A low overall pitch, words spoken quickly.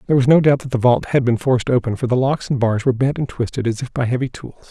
Yes: low, 125 Hz; fast, 320 wpm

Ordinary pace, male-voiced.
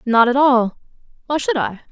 No: average, 190 wpm; female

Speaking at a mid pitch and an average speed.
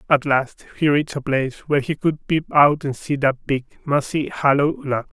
No: medium, 145 Hz; fast, 210 wpm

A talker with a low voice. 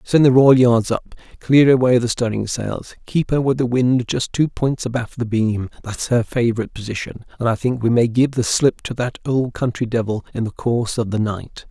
Yes: low, 120 Hz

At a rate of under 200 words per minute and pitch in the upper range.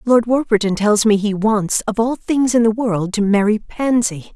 No: fast, 205 wpm; high, 220 Hz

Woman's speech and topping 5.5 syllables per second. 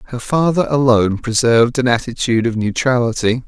No: male; 6.0 syllables/s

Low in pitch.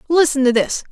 No: very high, 280 Hz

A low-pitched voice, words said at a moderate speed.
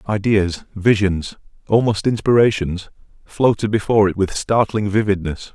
No: low, 100 Hz; slow, 110 wpm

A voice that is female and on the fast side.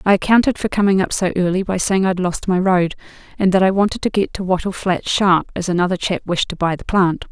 Yes: female; fast, 255 wpm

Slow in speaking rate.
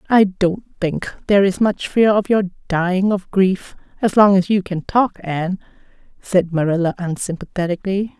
No: average, 160 wpm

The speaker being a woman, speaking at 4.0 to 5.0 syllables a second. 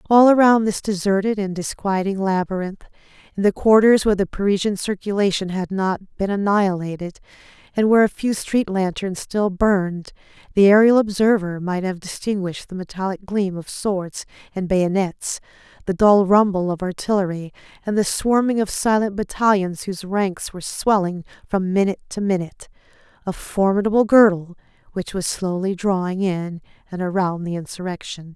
No: female; 5.2 syllables/s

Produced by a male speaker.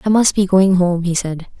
No: female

